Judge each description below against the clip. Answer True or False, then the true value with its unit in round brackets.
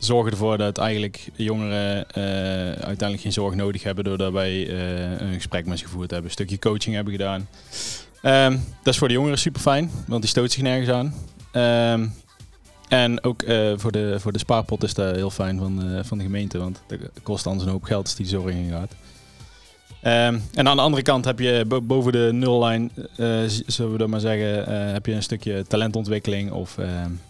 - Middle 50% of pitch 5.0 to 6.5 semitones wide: False (3.4 semitones)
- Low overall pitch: True (105 Hz)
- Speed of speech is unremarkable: False (205 wpm)